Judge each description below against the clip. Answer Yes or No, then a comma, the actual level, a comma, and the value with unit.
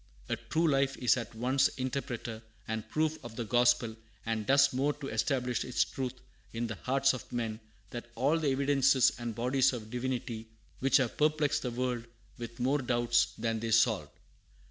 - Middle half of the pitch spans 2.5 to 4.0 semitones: Yes, average, 2.8 semitones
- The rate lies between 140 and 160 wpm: No, average, 175 wpm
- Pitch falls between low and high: No, low, 125 Hz